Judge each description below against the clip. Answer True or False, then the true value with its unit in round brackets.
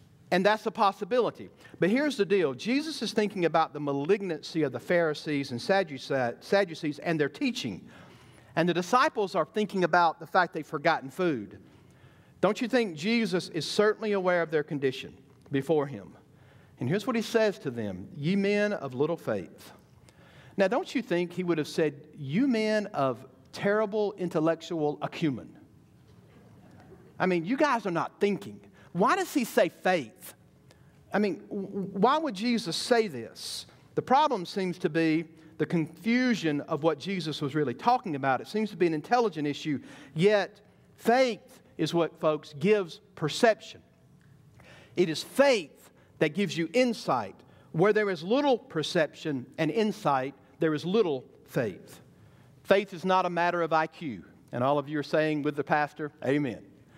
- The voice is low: False (170 Hz)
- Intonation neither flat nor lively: False (5.7 semitones)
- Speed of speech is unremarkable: True (160 wpm)